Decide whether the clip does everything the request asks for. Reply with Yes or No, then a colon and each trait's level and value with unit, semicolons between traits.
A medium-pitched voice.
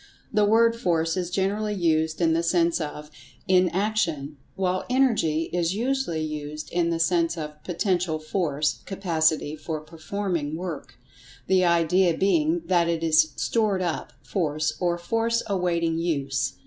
Yes: medium, 170 Hz